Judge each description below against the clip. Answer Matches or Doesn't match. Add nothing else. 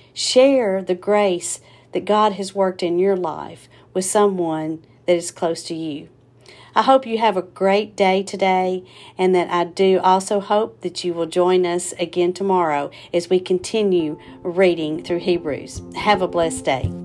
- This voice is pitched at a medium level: Matches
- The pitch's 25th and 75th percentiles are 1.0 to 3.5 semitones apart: Matches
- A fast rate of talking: Doesn't match